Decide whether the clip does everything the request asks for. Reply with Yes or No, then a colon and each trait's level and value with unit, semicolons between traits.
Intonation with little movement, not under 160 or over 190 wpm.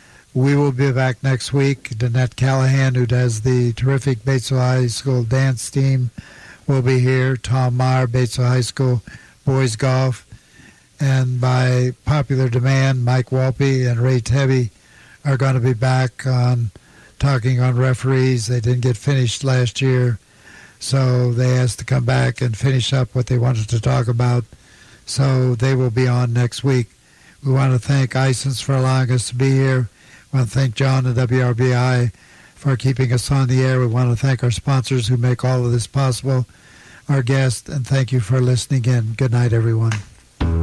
Yes: narrow, 1.3 semitones; average, 180 wpm